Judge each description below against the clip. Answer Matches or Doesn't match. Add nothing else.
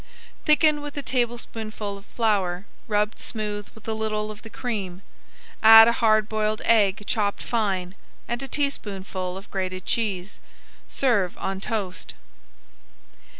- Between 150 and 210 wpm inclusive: Doesn't match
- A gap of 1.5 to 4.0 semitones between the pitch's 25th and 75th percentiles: Matches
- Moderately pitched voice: Doesn't match